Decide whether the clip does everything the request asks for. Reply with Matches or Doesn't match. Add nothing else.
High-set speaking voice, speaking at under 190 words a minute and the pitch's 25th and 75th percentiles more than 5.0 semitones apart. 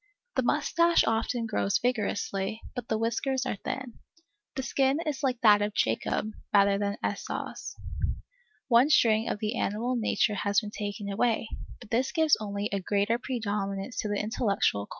Doesn't match